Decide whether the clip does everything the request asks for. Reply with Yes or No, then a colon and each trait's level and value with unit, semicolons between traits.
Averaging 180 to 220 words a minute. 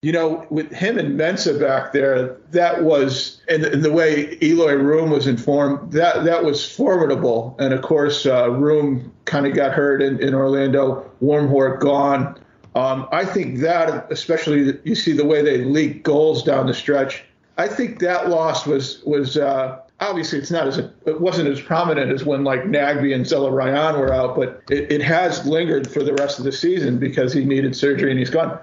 Yes: average, 195 wpm